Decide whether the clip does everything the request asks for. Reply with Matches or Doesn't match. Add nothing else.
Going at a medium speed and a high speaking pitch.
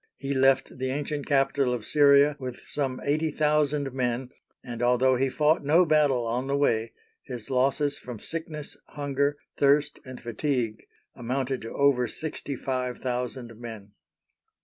Doesn't match